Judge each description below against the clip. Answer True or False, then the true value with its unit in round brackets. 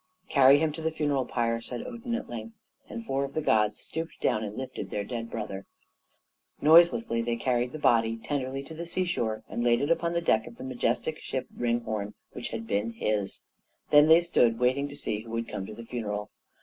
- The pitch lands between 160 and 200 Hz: False (125 Hz)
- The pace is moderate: False (210 wpm)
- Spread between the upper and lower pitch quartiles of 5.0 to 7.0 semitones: True (5.3 semitones)